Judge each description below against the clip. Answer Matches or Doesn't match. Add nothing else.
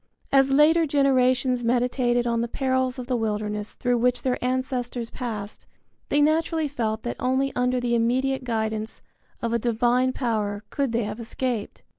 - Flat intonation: Matches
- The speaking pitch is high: Matches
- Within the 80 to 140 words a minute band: Doesn't match